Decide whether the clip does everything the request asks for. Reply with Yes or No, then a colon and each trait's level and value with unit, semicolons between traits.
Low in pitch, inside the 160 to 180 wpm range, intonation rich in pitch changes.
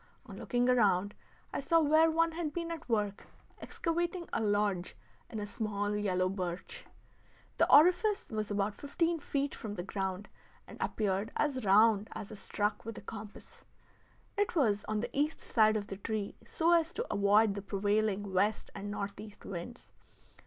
No: high, 215 Hz; average, 165 wpm; wide, 6.4 semitones